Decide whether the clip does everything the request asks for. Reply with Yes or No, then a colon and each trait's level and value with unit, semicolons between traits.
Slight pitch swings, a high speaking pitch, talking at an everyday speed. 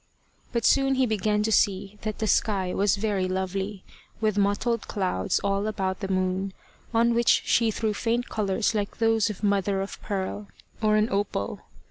Yes: narrow, 2.2 semitones; high, 205 Hz; average, 170 wpm